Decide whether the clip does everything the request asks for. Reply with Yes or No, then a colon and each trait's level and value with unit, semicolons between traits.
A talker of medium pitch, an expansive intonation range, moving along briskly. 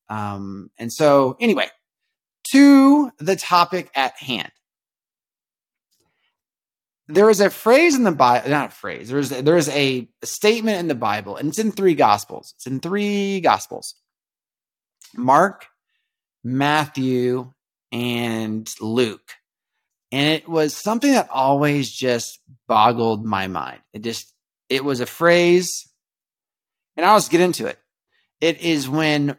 No: medium, 145 Hz; wide, 7.0 semitones; slow, 135 wpm